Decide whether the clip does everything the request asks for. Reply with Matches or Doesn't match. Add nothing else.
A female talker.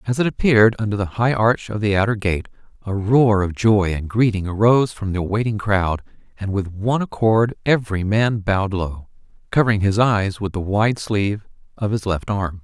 Doesn't match